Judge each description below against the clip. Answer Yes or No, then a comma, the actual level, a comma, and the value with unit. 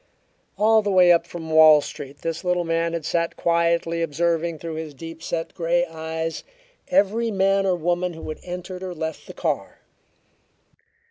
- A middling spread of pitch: No, narrow, 1.8 semitones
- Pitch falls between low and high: Yes, medium, 170 Hz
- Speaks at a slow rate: No, average, 165 wpm